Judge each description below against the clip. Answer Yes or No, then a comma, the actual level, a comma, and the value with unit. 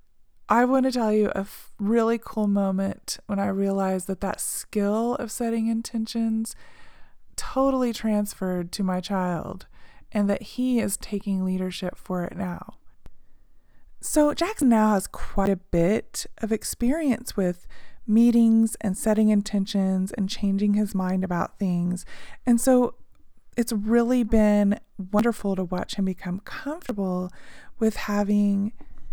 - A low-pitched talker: No, high, 205 Hz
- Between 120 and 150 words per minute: Yes, slow, 135 wpm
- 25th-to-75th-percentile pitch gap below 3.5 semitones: Yes, average, 3.1 semitones